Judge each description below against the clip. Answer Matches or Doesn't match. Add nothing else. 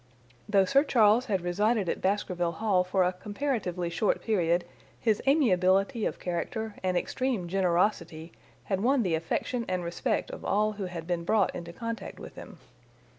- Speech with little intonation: Doesn't match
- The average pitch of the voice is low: Doesn't match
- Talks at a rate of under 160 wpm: Doesn't match